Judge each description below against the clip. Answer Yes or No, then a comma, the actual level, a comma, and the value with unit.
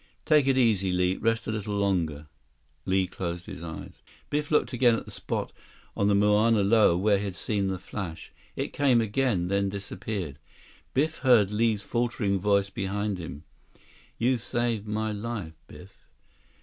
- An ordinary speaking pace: Yes, average, 160 wpm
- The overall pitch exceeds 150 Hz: No, low, 105 Hz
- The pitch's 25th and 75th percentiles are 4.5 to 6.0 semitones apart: No, average, 3.3 semitones